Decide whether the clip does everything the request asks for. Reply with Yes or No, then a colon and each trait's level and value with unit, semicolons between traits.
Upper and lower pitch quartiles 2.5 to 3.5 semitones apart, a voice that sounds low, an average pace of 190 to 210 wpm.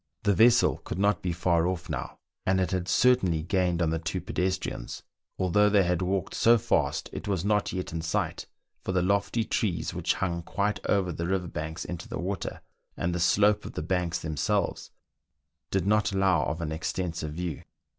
Yes: average, 2.9 semitones; very low, 90 Hz; average, 195 wpm